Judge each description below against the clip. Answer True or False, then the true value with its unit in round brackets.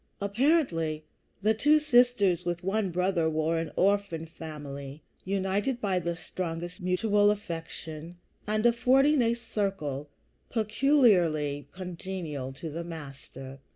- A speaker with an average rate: False (115 wpm)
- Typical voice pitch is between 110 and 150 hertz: False (180 Hz)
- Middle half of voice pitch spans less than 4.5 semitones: False (5.0 semitones)